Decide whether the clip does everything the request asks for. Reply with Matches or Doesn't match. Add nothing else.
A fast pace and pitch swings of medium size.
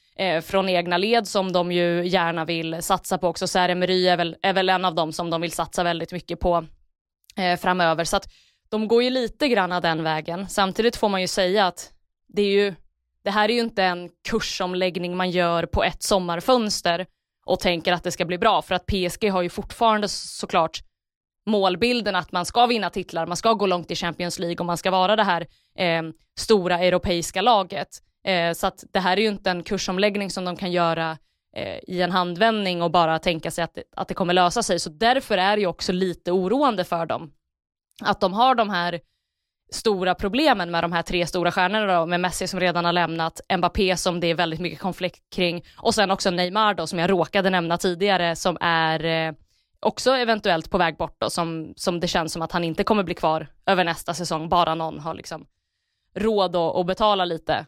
Doesn't match